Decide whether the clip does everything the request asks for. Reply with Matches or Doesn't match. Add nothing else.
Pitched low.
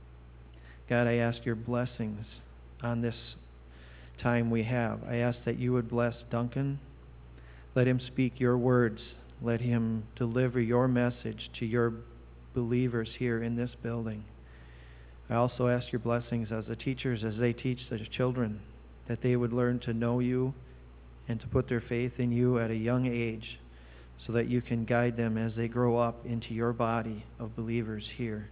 Matches